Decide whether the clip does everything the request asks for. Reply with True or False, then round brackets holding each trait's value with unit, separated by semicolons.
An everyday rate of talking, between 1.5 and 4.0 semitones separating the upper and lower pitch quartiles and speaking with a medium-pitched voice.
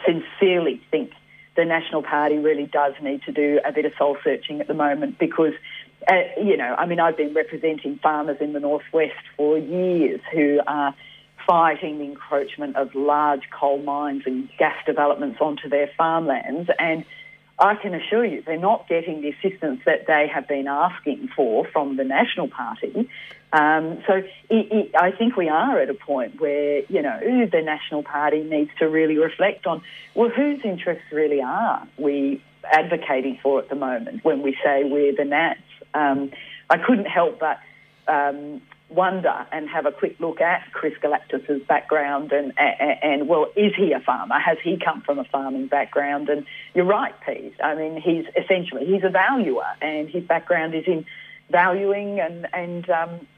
True (180 wpm; 3.4 semitones; 155 Hz)